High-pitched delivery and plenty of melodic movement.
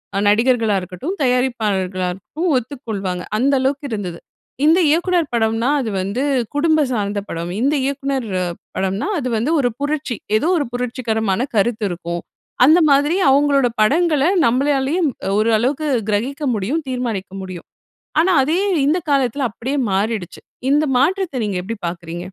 Yes: very high, 250 Hz; wide, 5.7 semitones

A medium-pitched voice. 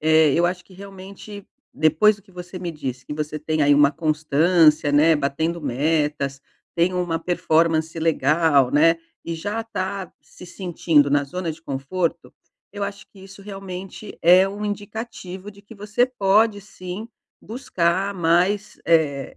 Yes: medium, 175 Hz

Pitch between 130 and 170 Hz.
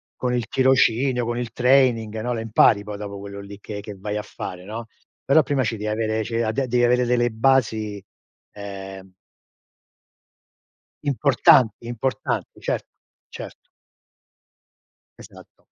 No: low, 115 Hz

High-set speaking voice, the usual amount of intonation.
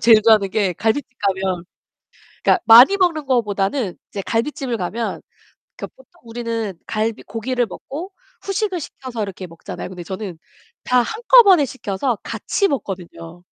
No: high, 225 Hz; wide, 6.0 semitones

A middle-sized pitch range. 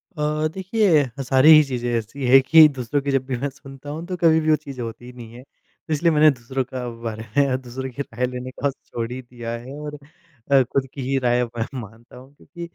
Yes: average, 3.5 semitones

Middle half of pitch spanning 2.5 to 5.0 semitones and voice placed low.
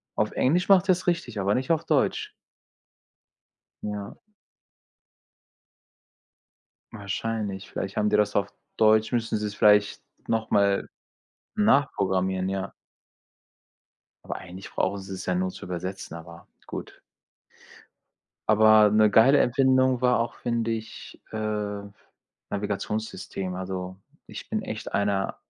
Yes: average, 2.8 semitones; low, 105 Hz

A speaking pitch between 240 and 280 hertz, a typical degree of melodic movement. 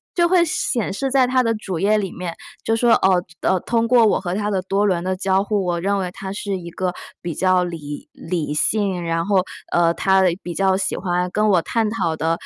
No: high, 190 Hz; average, 3.1 semitones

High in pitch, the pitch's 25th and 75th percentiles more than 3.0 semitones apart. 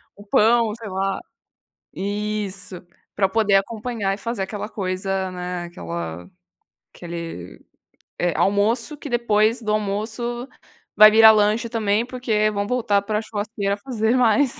No: high, 210 Hz; average, 2.7 semitones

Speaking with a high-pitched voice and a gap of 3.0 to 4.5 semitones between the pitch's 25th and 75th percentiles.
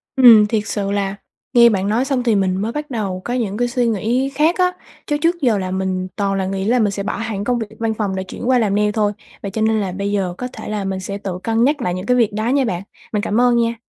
Yes: high, 215 Hz; average, 3.6 semitones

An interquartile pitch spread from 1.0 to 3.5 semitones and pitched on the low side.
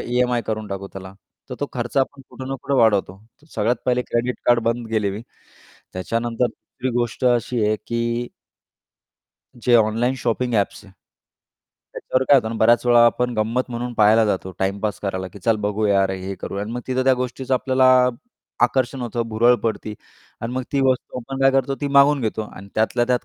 Yes: average, 2.8 semitones; low, 120 Hz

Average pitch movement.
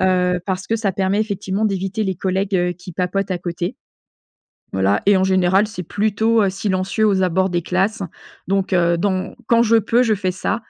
No: narrow, 2.1 semitones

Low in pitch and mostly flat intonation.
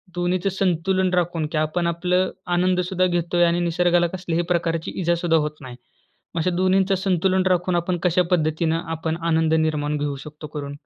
No: medium, 175 Hz; narrow, 2.2 semitones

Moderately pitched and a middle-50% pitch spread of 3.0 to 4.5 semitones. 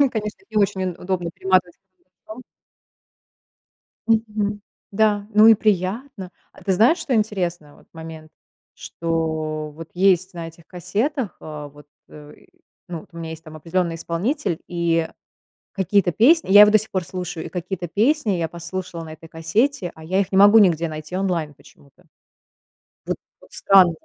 Yes: medium, 180 Hz; average, 4.1 semitones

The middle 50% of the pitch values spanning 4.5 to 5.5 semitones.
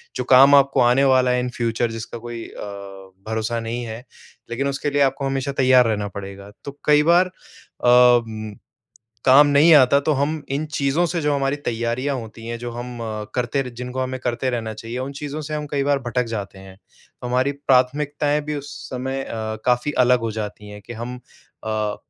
No: average, 3.2 semitones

